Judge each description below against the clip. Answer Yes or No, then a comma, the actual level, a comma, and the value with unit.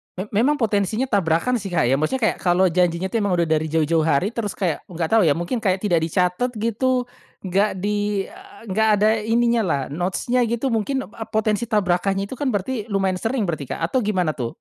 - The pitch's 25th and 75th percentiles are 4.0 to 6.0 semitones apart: Yes, average, 4.3 semitones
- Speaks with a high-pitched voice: Yes, high, 200 Hz